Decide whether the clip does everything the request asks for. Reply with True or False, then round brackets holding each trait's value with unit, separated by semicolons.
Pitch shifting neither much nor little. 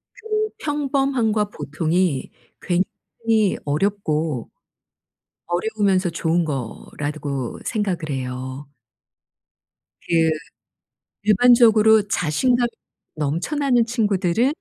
False (6.9 semitones)